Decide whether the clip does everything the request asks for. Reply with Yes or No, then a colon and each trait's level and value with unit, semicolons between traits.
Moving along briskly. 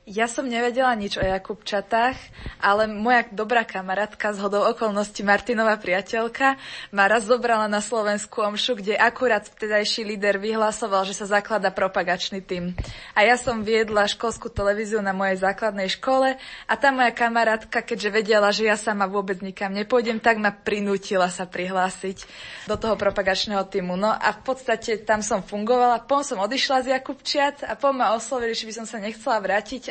Yes: fast, 170 wpm